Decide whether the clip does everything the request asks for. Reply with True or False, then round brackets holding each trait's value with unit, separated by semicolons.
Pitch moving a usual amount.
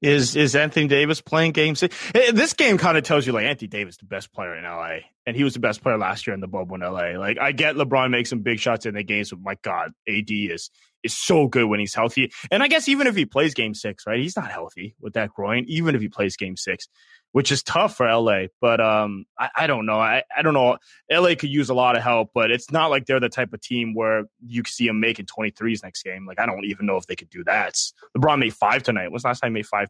False (5.9 semitones)